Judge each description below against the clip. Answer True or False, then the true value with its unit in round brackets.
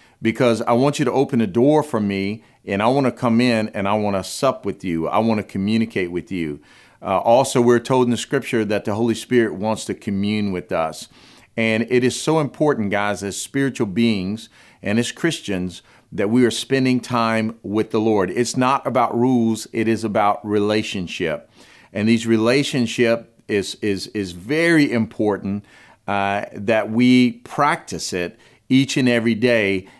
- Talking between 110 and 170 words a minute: False (180 wpm)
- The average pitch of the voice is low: True (115 Hz)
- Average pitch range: True (3.2 semitones)